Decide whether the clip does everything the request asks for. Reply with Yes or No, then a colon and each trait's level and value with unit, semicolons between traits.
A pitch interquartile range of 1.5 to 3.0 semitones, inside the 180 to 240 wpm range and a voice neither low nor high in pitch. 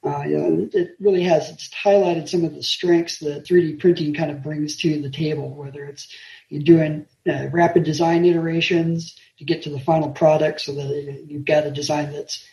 Yes: narrow, 2.4 semitones; average, 200 wpm; medium, 155 Hz